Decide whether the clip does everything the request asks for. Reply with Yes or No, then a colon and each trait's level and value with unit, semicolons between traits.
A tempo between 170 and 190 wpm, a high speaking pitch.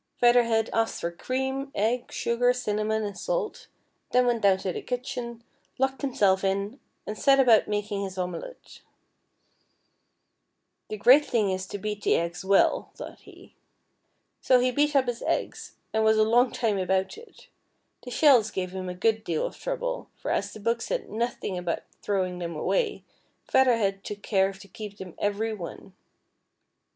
Yes: average, 175 wpm; high, 220 Hz